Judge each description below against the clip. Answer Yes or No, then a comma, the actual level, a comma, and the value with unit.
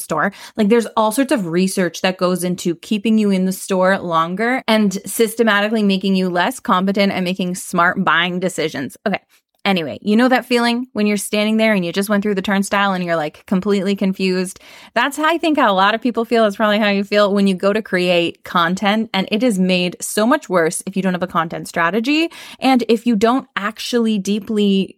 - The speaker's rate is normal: No, fast, 215 wpm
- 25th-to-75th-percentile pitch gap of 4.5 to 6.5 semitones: No, average, 3.6 semitones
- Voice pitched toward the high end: Yes, high, 200 Hz